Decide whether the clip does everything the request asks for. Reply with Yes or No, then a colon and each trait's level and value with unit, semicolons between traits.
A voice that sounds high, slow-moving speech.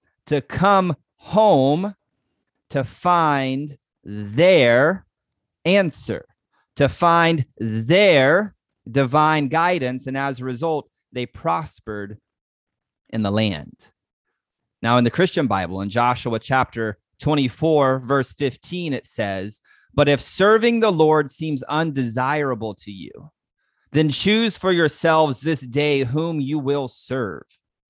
No: medium, 140 Hz; slow, 115 wpm